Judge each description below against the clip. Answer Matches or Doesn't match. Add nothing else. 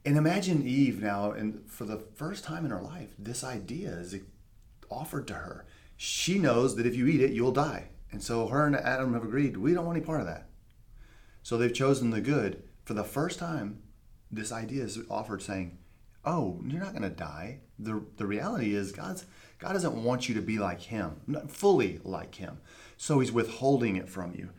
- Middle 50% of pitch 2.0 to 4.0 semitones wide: Doesn't match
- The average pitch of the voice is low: Matches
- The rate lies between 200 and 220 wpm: Matches